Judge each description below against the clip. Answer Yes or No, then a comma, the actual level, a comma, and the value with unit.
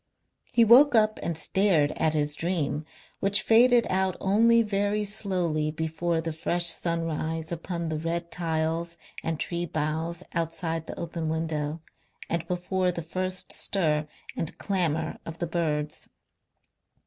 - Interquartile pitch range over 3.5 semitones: No, average, 2.7 semitones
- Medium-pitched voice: Yes, medium, 170 Hz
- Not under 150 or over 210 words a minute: No, average, 140 wpm